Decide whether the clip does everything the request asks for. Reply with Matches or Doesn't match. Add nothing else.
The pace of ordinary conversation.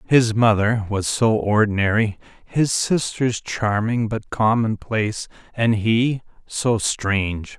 Doesn't match